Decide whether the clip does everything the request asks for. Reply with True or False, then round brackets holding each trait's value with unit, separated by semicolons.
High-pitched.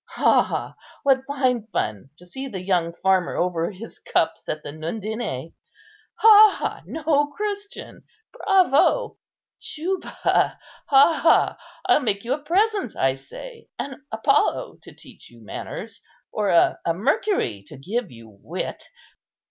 True (240 Hz)